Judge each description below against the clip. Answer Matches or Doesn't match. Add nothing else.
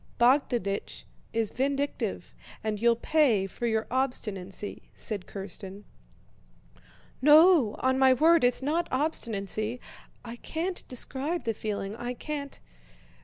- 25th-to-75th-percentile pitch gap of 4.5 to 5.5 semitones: Matches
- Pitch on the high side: Matches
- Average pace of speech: Doesn't match